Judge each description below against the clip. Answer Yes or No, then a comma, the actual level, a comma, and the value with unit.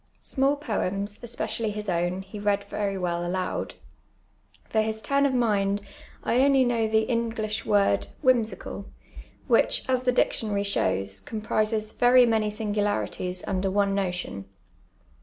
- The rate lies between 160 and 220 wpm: No, average, 140 wpm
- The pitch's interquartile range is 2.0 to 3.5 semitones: Yes, average, 2.8 semitones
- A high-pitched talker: Yes, high, 210 Hz